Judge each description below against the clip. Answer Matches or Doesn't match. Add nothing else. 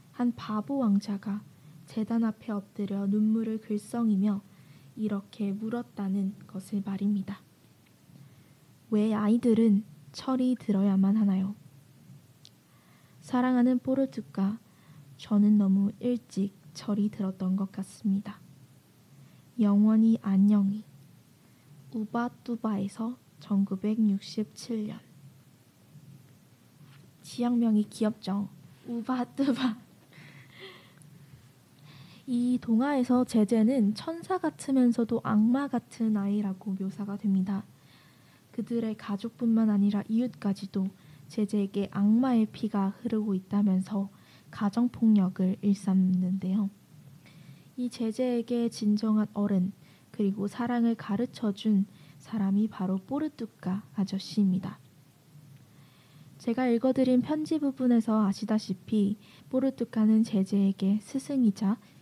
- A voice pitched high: Matches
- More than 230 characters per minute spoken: Doesn't match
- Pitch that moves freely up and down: Doesn't match